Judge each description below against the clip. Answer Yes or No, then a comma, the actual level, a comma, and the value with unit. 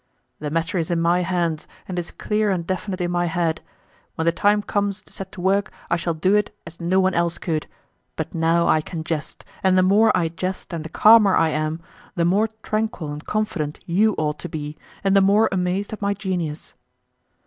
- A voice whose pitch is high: No, medium, 180 Hz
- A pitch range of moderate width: Yes, average, 3.2 semitones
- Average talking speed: No, fast, 215 wpm